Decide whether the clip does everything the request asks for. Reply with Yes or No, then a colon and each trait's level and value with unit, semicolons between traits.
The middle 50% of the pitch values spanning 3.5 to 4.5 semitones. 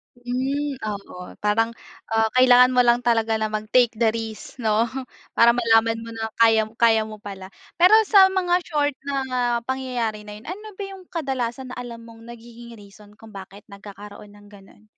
No: average, 2.8 semitones